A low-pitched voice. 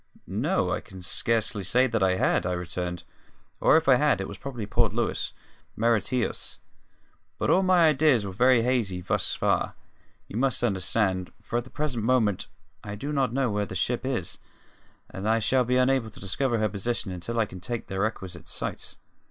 Yes: low, 115 Hz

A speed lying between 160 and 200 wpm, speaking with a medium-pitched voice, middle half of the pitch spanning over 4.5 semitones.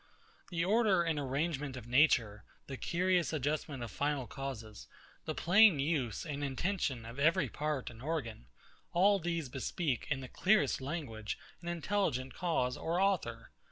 No: average, 150 wpm; medium, 145 Hz; average, 5.1 semitones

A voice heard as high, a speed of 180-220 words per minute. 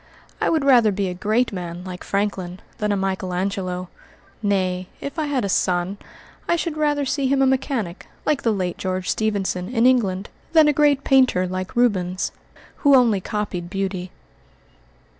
No: high, 200 Hz; average, 170 wpm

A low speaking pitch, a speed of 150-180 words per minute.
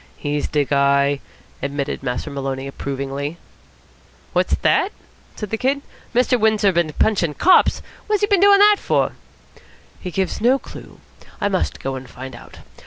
No: medium, 155 Hz; average, 155 wpm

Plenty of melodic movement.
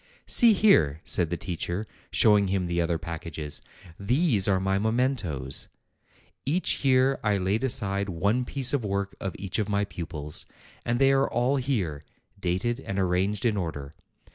Yes: wide, 5.8 semitones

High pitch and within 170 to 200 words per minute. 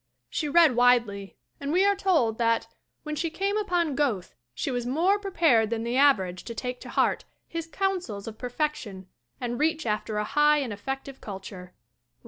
Yes: very high, 260 Hz; average, 175 wpm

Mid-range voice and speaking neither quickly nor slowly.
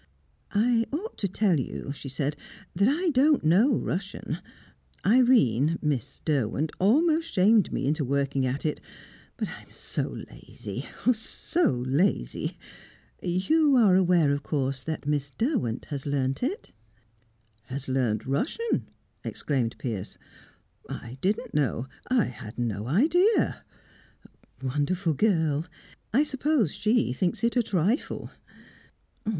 No: medium, 170 Hz; slow, 130 wpm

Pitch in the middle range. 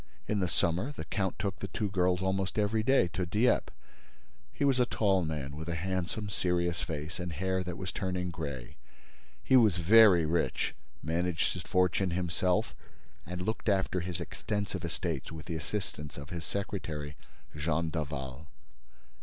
No: very low, 90 Hz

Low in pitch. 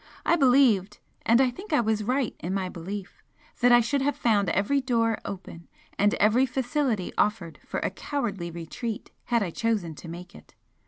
No: high, 220 Hz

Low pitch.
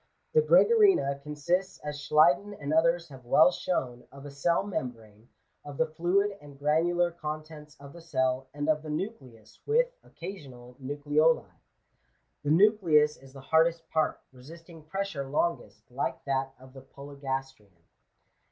No: medium, 150 Hz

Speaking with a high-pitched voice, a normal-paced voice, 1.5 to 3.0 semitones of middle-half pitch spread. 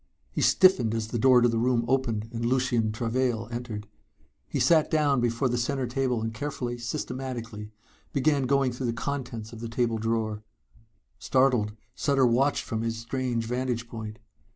No: low, 120 Hz; average, 165 wpm; narrow, 2.4 semitones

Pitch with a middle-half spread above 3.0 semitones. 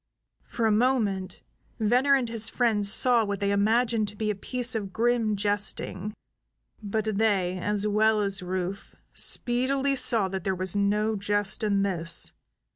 No: narrow, 2.5 semitones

